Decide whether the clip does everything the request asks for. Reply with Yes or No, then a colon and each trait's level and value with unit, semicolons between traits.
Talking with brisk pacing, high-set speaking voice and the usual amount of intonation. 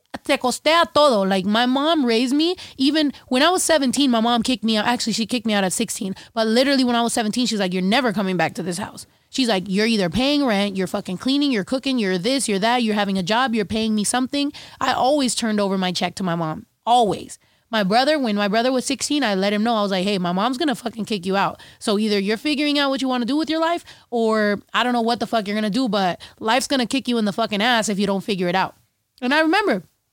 Yes: fast, 270 wpm; high, 230 Hz; average, 4.4 semitones